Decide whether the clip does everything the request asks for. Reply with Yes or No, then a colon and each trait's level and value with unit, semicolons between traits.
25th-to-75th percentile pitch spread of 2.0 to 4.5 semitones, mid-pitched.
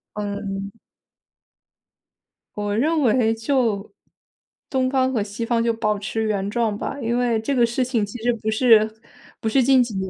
No: average, 2.9 semitones; high, 225 Hz